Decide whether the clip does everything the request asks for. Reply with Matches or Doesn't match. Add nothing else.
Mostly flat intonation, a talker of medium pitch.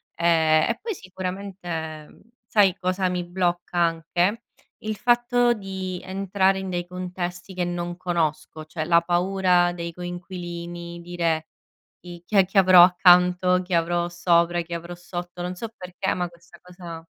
Matches